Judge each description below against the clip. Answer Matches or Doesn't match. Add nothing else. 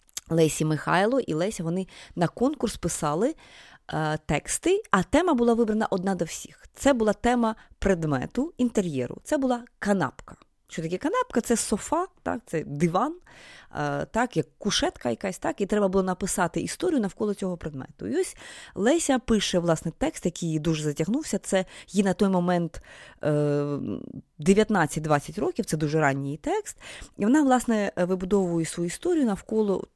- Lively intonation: Matches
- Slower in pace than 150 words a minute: Doesn't match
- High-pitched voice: Matches